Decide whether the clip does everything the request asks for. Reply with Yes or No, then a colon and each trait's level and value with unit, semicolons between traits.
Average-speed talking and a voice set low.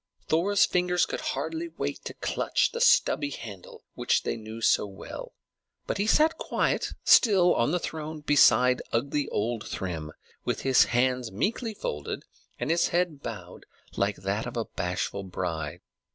Yes: average, 150 wpm; low, 125 Hz